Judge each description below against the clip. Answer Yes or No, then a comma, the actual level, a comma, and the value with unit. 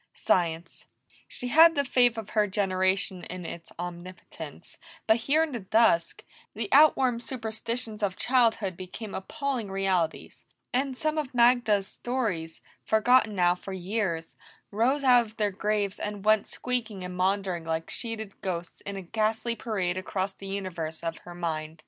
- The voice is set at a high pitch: Yes, high, 205 Hz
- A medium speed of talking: Yes, average, 155 wpm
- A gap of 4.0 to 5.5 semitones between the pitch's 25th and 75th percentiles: Yes, average, 4.6 semitones